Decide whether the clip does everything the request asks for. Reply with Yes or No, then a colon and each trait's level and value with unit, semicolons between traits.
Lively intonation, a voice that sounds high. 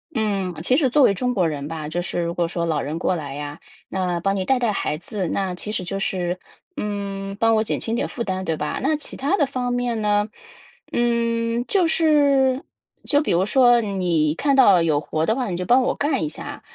Yes: wide, 6.1 semitones; high, 200 Hz